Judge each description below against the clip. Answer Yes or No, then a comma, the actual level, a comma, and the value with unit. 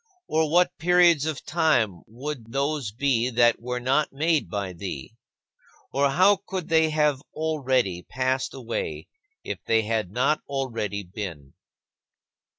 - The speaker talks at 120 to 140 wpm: Yes, slow, 135 wpm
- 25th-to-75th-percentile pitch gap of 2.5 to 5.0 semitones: No, wide, 5.5 semitones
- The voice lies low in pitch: Yes, low, 130 Hz